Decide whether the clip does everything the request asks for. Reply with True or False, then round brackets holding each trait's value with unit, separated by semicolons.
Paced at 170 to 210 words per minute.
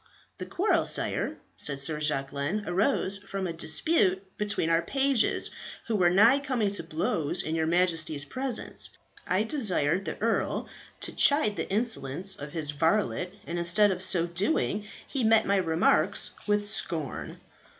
False (150 wpm)